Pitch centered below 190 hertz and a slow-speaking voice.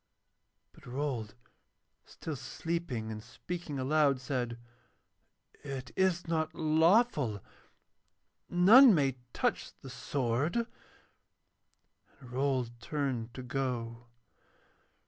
Yes: medium, 140 Hz; slow, 90 wpm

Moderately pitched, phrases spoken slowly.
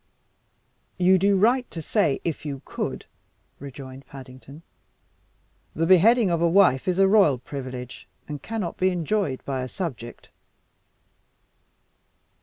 Yes: medium, 165 Hz; slow, 125 wpm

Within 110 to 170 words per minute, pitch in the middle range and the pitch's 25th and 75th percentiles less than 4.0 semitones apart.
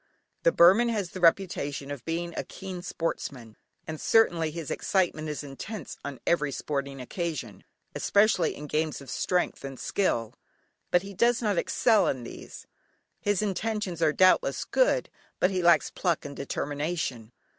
No: average, 155 wpm; medium, 170 Hz; average, 5.1 semitones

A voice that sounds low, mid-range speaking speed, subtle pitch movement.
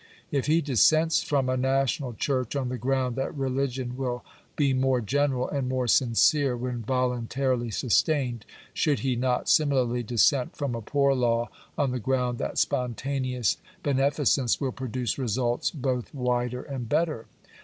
Yes: low, 130 Hz; average, 155 wpm; narrow, 1.9 semitones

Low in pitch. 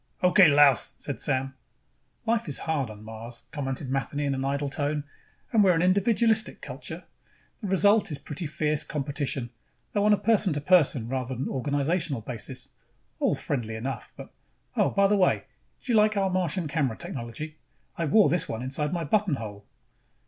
No: medium, 150 Hz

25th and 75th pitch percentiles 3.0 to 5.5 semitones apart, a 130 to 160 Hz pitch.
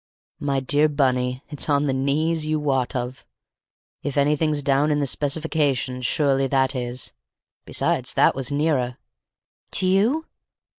No: narrow, 2.4 semitones; medium, 140 Hz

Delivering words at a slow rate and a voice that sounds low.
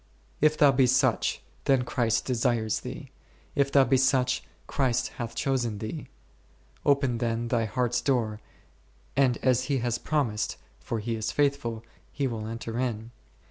No: average, 155 wpm; low, 125 Hz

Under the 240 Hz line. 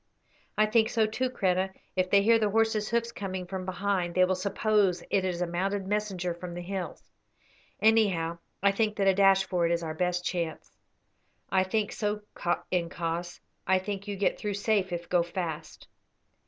Yes: high, 190 Hz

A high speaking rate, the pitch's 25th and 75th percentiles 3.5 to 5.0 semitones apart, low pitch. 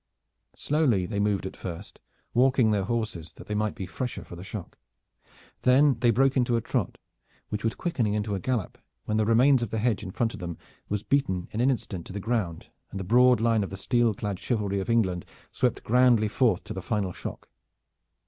Yes: fast, 215 wpm; average, 4.0 semitones; low, 110 Hz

